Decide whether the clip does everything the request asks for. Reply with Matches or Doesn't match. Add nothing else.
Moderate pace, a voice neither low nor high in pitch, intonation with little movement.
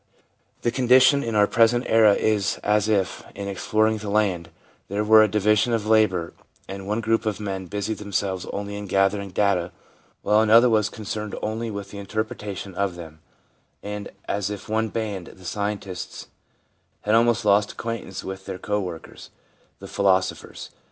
Doesn't match